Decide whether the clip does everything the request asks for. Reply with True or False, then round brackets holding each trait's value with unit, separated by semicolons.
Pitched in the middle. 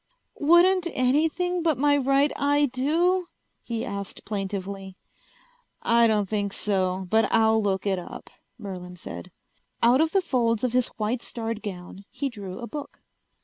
False (230 Hz)